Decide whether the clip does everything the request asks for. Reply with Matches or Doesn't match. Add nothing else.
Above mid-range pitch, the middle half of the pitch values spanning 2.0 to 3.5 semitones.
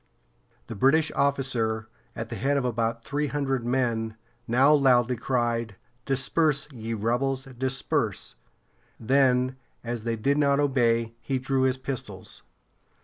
Doesn't match